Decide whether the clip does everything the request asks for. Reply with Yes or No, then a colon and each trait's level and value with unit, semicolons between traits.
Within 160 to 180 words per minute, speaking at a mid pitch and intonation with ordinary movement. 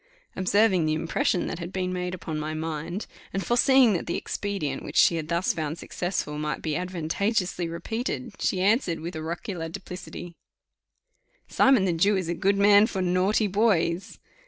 Yes: average, 165 wpm; medium, 180 Hz; average, 3.4 semitones